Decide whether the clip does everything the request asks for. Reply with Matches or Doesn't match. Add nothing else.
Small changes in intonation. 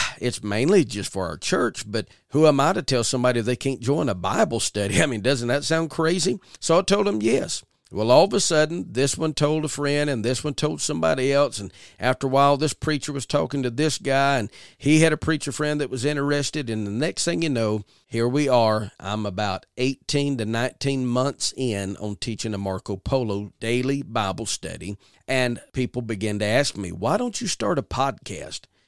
Doesn't match